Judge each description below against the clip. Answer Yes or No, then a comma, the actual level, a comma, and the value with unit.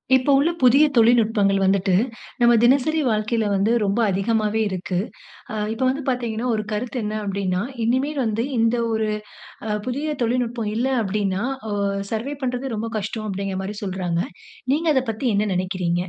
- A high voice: Yes, high, 220 Hz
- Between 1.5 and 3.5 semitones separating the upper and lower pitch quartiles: No, average, 3.9 semitones